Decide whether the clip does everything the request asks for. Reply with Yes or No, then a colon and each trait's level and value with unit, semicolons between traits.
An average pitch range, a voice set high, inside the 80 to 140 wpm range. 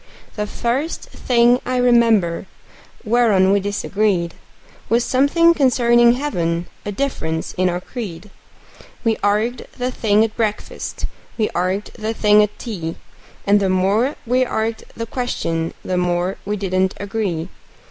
Yes: average, 4.2 semitones; high, 210 Hz; slow, 135 wpm